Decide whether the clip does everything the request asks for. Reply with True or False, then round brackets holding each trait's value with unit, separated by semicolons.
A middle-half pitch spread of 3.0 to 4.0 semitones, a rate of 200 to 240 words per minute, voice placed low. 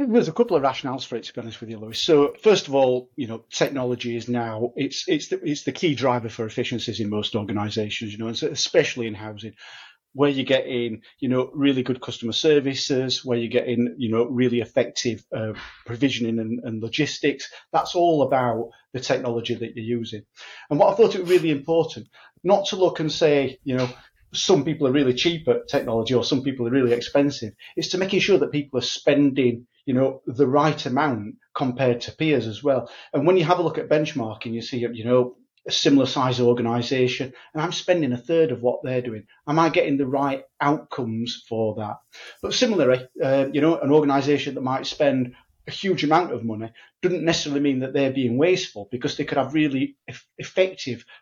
True (3.7 semitones; 205 wpm; 130 Hz)